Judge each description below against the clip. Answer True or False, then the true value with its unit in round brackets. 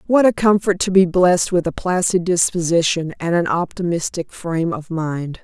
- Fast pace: False (175 wpm)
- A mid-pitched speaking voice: True (175 Hz)